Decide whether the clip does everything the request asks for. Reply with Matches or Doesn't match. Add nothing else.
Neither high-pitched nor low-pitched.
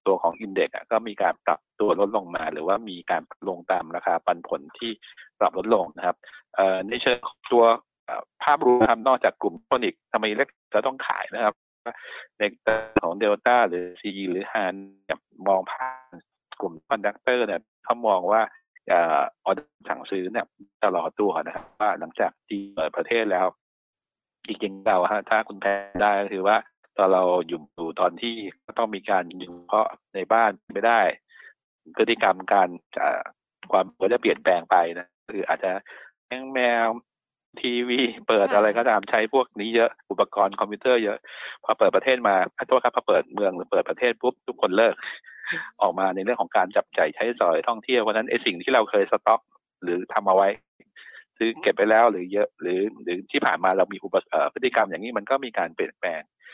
Doesn't match